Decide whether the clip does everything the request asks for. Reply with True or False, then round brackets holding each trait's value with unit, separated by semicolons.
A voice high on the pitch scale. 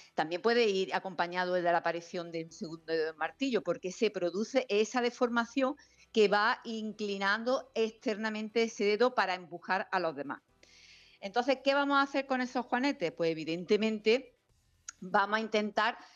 True (210 Hz)